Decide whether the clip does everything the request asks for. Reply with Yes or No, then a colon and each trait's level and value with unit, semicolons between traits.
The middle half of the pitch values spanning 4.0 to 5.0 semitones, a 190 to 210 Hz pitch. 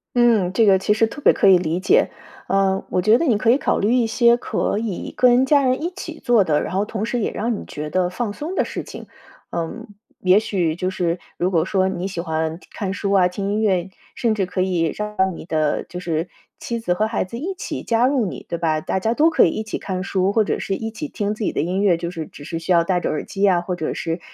Yes: average, 4.4 semitones; high, 195 Hz